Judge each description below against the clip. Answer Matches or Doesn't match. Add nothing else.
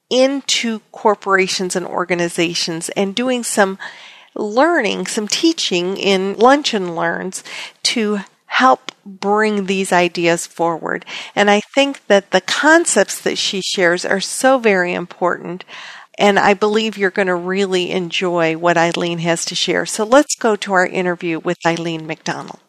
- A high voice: Matches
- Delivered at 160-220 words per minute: Doesn't match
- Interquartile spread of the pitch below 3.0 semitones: Doesn't match